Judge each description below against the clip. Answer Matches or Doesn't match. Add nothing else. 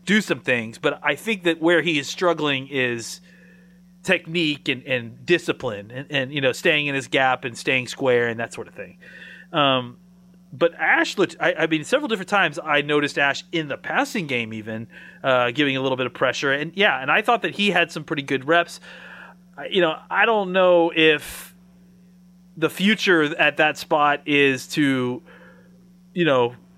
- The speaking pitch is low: Doesn't match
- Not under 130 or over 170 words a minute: Doesn't match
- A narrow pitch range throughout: Doesn't match